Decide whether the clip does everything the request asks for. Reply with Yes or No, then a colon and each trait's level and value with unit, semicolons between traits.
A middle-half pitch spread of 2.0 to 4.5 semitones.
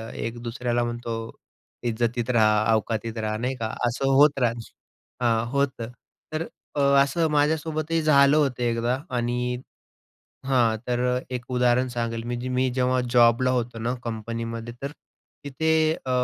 Yes: average, 2.7 semitones